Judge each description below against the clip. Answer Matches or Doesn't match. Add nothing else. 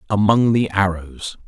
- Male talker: Matches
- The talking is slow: Matches